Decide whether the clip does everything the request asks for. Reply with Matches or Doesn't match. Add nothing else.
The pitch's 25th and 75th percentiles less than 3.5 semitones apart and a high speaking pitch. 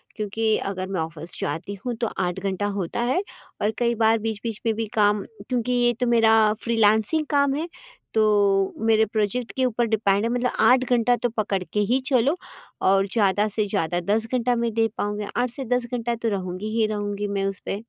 Matches